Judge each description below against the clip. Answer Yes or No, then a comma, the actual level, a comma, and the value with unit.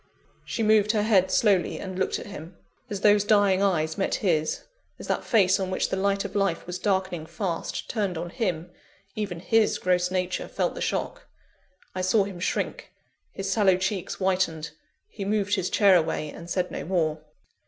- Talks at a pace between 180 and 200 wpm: Yes, average, 185 wpm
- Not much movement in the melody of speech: Yes, narrow, 2.3 semitones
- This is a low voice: No, high, 190 Hz